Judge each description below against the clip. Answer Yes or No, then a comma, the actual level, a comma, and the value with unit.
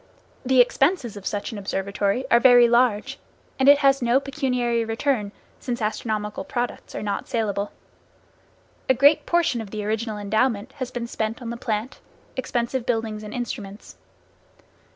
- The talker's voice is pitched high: Yes, high, 235 Hz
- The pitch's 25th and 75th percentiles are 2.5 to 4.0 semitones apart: Yes, average, 3.4 semitones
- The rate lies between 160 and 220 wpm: No, average, 150 wpm